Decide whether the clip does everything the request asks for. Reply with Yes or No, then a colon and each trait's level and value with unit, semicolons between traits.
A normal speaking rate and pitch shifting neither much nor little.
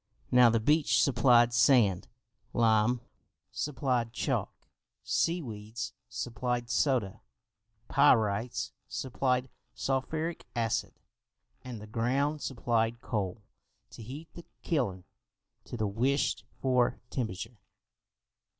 No: slow, 95 wpm; average, 3.1 semitones